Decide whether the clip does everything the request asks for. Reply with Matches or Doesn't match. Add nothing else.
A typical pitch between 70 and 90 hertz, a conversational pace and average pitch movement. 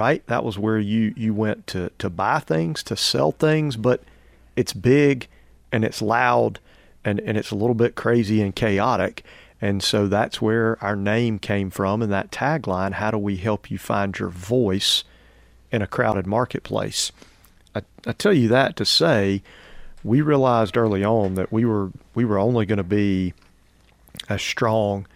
Doesn't match